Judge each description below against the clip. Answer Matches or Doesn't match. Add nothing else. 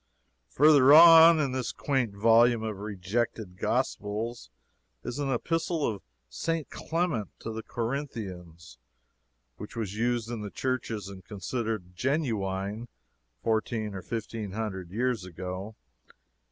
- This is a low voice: Matches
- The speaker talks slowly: Matches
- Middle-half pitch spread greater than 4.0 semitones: Matches